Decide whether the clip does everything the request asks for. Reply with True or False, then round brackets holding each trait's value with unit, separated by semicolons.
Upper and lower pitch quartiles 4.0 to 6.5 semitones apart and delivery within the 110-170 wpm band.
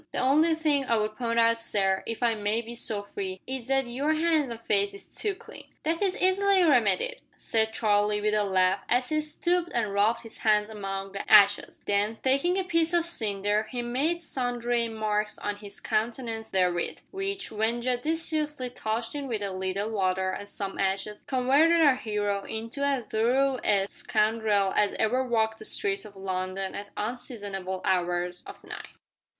False (4.7 semitones; 180 wpm)